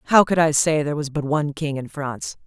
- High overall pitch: No, medium, 150 Hz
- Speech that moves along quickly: Yes, fast, 270 wpm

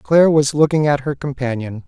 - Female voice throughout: No, male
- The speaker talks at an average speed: Yes, average, 190 wpm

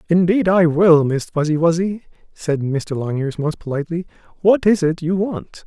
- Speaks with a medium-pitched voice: Yes, medium, 170 Hz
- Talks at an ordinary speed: Yes, average, 170 wpm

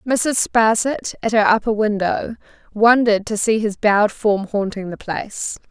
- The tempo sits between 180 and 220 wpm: No, average, 160 wpm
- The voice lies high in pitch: Yes, high, 215 Hz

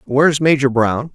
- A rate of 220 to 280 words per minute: No, fast, 210 wpm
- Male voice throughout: Yes, male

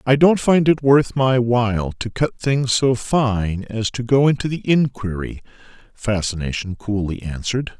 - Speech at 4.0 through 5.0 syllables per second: Yes, 4.4 syllables/s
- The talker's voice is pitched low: Yes, low, 120 Hz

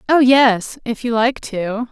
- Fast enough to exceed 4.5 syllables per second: No, 3.6 syllables/s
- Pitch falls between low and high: No, high, 240 Hz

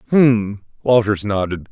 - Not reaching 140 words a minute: Yes, slow, 105 wpm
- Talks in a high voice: No, low, 110 Hz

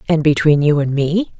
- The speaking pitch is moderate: Yes, medium, 155 Hz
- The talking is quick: Yes, fast, 215 wpm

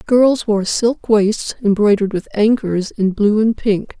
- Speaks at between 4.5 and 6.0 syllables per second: No, 4.0 syllables/s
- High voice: Yes, high, 215 Hz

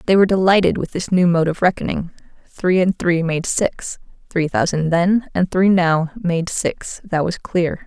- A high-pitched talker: No, medium, 175 Hz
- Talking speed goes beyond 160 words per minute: Yes, average, 190 wpm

